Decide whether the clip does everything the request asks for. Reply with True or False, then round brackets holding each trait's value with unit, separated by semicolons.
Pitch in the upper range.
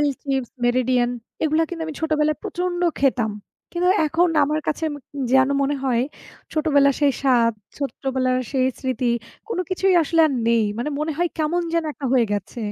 True (280 Hz)